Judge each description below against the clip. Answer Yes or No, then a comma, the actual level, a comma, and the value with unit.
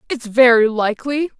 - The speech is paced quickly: No, slow, 130 wpm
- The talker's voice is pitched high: Yes, high, 245 Hz